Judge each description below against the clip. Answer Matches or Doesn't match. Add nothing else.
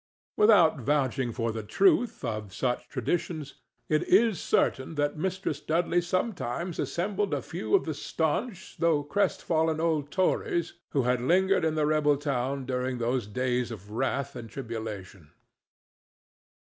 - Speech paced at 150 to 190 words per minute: Doesn't match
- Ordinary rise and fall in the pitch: Doesn't match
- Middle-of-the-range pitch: Matches